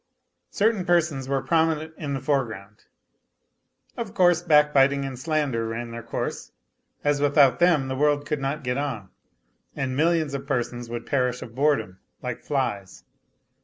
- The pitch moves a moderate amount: Yes, average, 3.4 semitones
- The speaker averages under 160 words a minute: Yes, average, 150 wpm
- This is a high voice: No, medium, 140 Hz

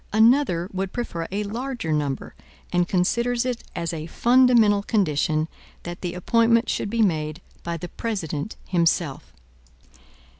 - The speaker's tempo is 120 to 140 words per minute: Yes, slow, 135 wpm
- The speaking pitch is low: No, high, 190 Hz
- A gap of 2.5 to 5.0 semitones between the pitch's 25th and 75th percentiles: No, wide, 5.6 semitones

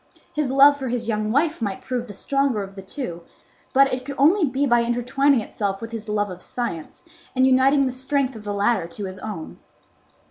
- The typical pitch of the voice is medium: No, high, 240 Hz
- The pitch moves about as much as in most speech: Yes, average, 4.8 semitones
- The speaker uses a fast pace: Yes, fast, 210 wpm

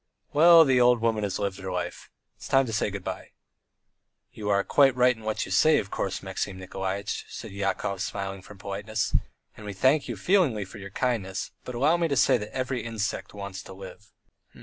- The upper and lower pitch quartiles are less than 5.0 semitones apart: Yes, average, 4.4 semitones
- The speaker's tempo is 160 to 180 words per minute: No, average, 200 wpm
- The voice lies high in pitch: No, low, 105 Hz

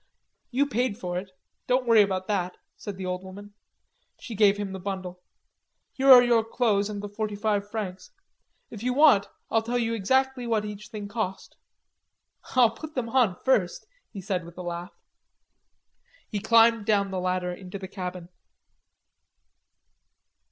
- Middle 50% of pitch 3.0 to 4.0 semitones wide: Yes, average, 3.6 semitones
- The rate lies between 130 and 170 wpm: Yes, average, 160 wpm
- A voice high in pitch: Yes, high, 205 Hz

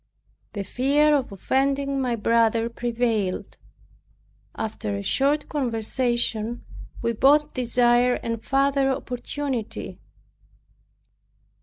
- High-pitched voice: Yes, high, 245 Hz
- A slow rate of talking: Yes, slow, 90 wpm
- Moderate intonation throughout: Yes, average, 3.1 semitones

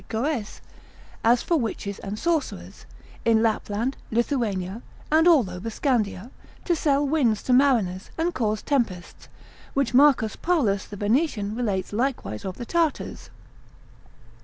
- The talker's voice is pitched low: No, high, 235 Hz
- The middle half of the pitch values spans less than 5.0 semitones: No, wide, 5.5 semitones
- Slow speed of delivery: Yes, slow, 130 wpm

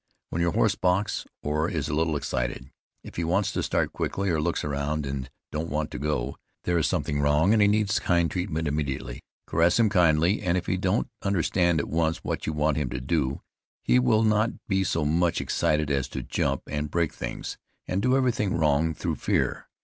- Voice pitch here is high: No, very low, 80 Hz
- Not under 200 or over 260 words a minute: Yes, fast, 205 wpm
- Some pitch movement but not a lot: Yes, average, 3.7 semitones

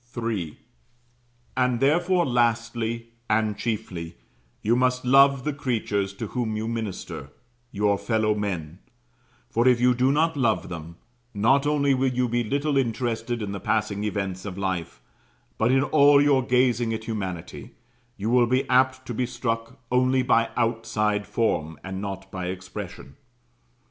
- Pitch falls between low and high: No, low, 115 Hz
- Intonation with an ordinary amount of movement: Yes, average, 3.8 semitones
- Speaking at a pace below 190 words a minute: Yes, average, 150 wpm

